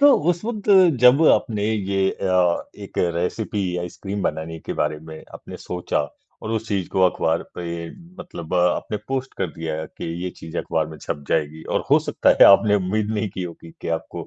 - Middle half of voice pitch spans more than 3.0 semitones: Yes, average, 4.5 semitones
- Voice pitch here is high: No, very low, 90 Hz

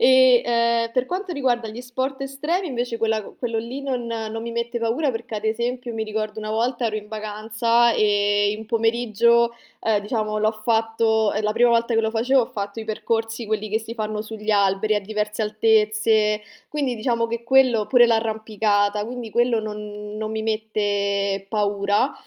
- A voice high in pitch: Yes, high, 225 Hz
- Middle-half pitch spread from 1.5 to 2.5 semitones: Yes, narrow, 1.9 semitones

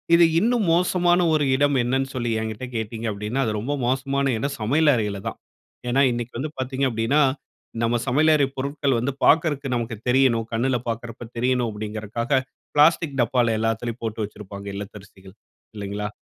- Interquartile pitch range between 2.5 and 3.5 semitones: No, average, 3.9 semitones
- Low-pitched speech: Yes, low, 120 Hz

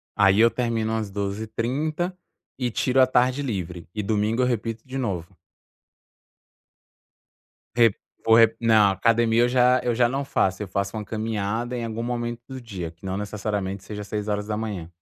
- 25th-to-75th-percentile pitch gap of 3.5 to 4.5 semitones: No, average, 2.9 semitones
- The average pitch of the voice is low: Yes, low, 110 Hz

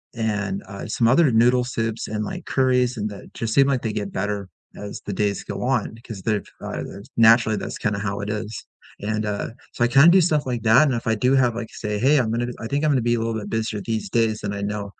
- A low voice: Yes, low, 115 Hz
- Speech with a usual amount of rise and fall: Yes, average, 3.0 semitones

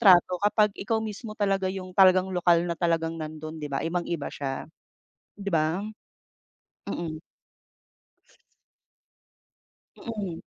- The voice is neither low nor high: Yes, medium, 180 Hz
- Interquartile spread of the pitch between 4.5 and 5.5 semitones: No, average, 3.4 semitones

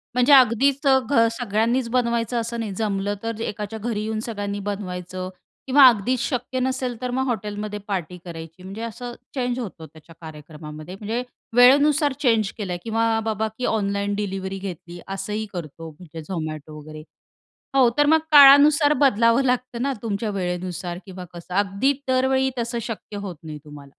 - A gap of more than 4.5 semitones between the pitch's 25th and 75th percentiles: Yes, average, 5.2 semitones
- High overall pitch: Yes, high, 215 Hz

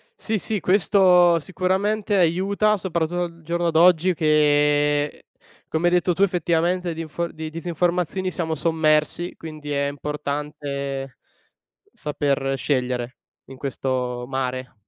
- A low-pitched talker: No, medium, 160 Hz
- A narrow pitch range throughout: No, average, 3.5 semitones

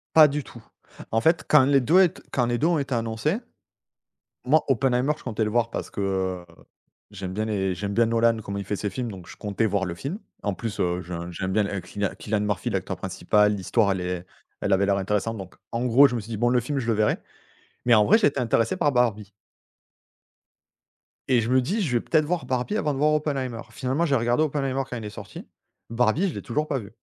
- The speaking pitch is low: Yes, low, 115 Hz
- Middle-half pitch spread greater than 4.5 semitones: Yes, average, 4.9 semitones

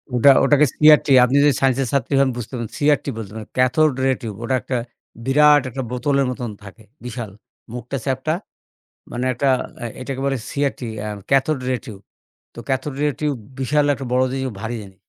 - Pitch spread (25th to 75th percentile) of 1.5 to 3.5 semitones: Yes, narrow, 2.6 semitones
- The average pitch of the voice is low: Yes, low, 130 Hz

